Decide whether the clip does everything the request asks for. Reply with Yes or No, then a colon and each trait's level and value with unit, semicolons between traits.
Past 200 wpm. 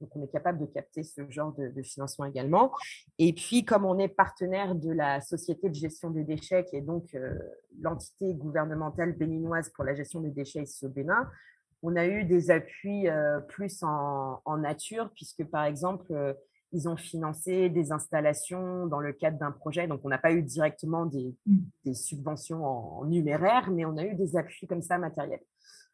No: average, 195 wpm